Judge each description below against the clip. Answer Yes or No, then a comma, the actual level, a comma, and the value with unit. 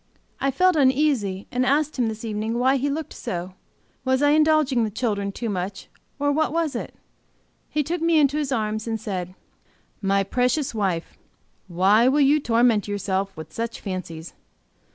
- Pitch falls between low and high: No, high, 235 Hz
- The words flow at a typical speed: Yes, average, 170 wpm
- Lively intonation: Yes, wide, 6.3 semitones